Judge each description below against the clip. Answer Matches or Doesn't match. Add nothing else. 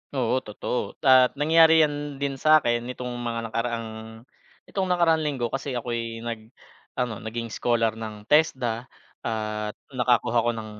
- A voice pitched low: Matches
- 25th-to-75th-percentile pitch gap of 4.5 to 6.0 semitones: Doesn't match